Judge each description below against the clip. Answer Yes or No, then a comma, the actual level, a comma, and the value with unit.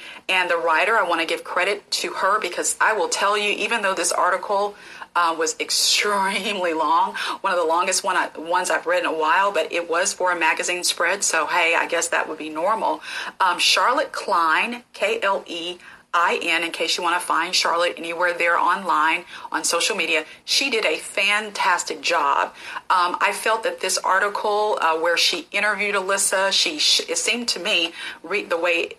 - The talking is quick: No, average, 190 wpm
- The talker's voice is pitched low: No, high, 205 Hz